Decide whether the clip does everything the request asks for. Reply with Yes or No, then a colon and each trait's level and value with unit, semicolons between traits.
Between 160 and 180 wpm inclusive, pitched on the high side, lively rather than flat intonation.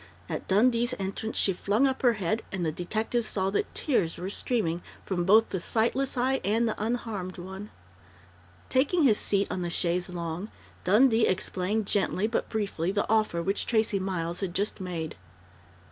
No: average, 170 wpm; high, 200 Hz; average, 3.8 semitones